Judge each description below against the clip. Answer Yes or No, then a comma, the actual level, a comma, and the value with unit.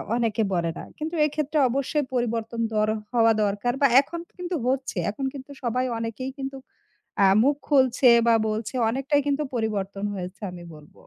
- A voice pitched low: No, high, 245 Hz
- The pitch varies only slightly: No, average, 4.3 semitones